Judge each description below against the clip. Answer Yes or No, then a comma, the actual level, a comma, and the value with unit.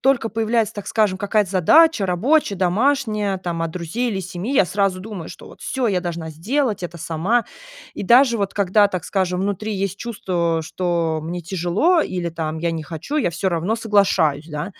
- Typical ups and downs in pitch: Yes, average, 4.3 semitones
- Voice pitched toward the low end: No, high, 190 Hz